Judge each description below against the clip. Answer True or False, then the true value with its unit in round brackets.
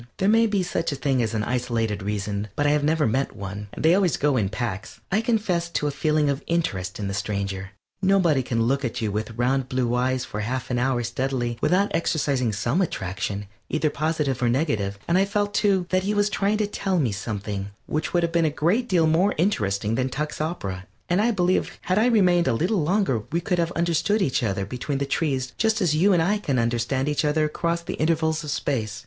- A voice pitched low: False (145 Hz)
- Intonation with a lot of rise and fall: True (7.1 semitones)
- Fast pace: True (225 wpm)